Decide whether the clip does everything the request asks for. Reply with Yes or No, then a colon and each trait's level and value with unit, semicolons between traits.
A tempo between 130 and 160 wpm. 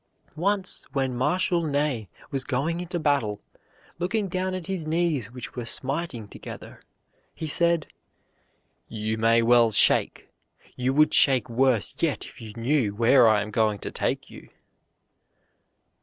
Yes: average, 140 wpm